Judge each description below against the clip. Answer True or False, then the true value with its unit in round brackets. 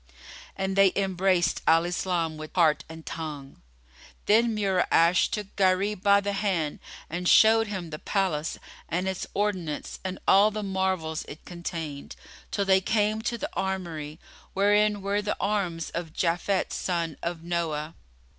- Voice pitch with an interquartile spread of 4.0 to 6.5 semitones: False (3.4 semitones)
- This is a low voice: False (185 Hz)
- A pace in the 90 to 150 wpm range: True (145 wpm)